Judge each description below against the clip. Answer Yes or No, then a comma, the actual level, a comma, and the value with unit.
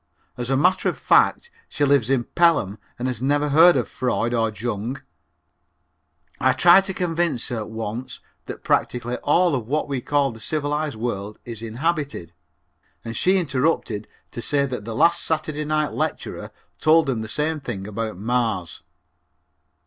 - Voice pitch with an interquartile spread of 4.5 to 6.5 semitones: Yes, average, 5.2 semitones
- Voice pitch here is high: No, low, 130 Hz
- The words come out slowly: No, average, 160 wpm